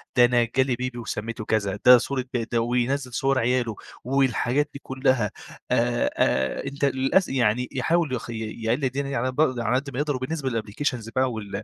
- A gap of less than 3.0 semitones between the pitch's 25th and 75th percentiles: Yes, narrow, 2.4 semitones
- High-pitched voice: No, low, 125 Hz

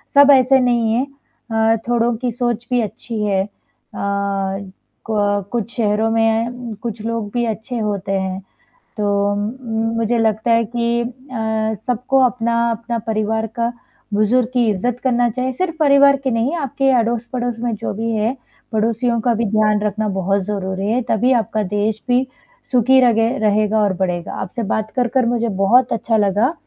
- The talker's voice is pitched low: No, high, 225 Hz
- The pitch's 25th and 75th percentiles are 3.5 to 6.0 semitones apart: No, narrow, 2.4 semitones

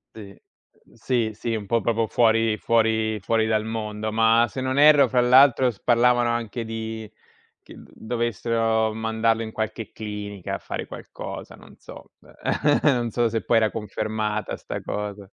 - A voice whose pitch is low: Yes, low, 110 Hz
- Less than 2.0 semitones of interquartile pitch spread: Yes, narrow, 1.5 semitones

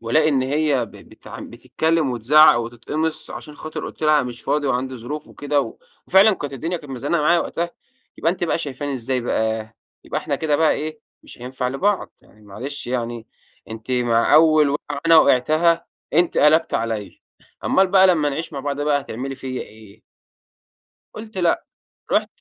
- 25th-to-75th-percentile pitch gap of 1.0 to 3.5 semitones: No, average, 4.2 semitones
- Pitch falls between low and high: Yes, medium, 145 Hz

